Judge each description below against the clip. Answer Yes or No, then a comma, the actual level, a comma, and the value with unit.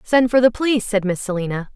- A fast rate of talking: Yes, fast, 240 wpm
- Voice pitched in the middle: No, high, 220 Hz